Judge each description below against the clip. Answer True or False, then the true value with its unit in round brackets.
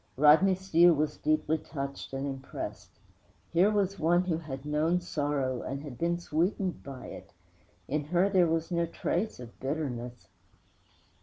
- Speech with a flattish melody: False (4.0 semitones)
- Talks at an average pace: True (150 wpm)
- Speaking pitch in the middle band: True (155 Hz)